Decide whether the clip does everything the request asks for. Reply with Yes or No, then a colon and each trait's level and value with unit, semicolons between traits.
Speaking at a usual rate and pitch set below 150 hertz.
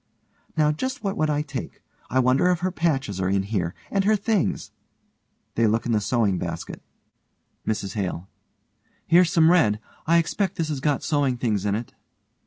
Yes: average, 180 wpm; low, 135 Hz